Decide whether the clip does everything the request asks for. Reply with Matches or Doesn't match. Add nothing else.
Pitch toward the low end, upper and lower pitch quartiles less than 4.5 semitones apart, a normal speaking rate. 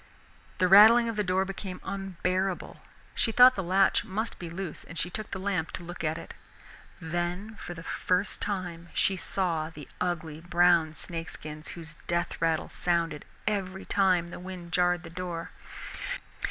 Doesn't match